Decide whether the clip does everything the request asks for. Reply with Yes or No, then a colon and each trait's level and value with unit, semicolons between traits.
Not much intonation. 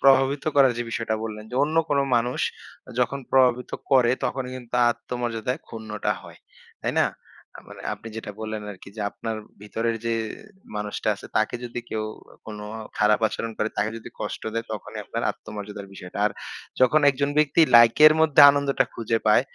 No: average, 3.4 semitones